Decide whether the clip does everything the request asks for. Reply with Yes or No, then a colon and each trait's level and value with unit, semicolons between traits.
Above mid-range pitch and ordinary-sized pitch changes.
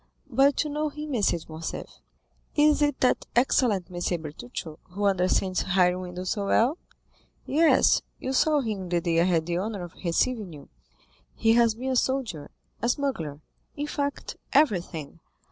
No: high, 205 Hz; wide, 7.4 semitones